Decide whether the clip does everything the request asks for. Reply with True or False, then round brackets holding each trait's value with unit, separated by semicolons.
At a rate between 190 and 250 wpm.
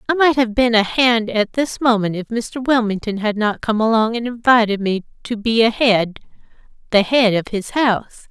True (195 wpm)